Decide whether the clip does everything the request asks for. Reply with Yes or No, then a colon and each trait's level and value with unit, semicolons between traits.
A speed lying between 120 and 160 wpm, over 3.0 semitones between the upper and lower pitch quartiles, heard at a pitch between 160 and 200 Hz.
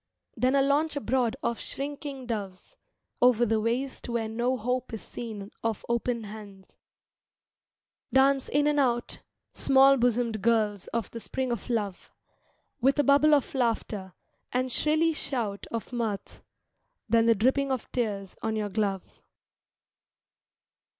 No: slow, 135 wpm; average, 3.5 semitones; high, 235 Hz